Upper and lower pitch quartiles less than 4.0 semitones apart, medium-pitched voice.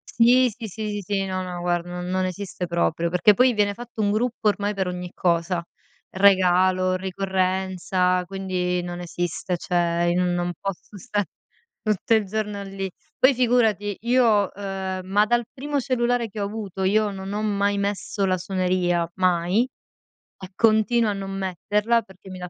No: average, 2.7 semitones; high, 195 Hz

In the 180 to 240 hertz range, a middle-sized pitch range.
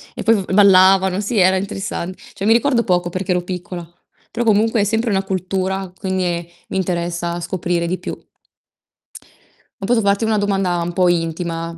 No: high, 190 Hz; narrow, 2.3 semitones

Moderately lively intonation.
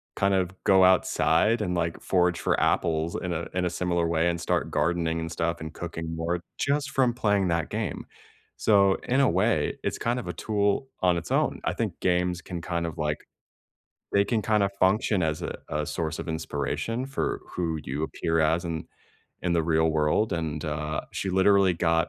Yes: average, 3.2 semitones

